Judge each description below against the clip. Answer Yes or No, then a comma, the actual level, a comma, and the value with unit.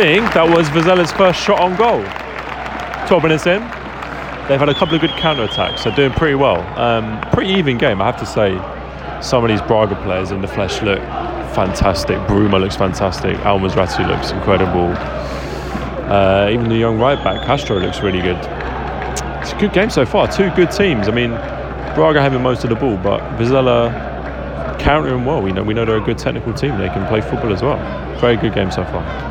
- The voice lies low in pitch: Yes, low, 115 Hz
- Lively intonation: Yes, wide, 6.8 semitones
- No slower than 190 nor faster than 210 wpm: Yes, average, 200 wpm